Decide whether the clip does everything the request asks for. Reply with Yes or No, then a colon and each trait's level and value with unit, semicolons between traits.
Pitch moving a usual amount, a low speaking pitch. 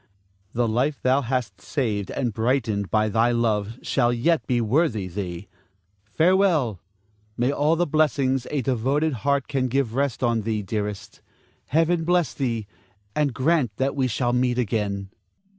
Yes: average, 4.5 semitones; low, 125 Hz